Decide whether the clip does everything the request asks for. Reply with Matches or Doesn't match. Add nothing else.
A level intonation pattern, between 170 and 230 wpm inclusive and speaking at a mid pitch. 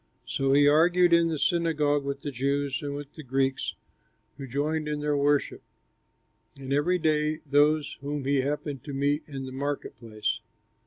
Matches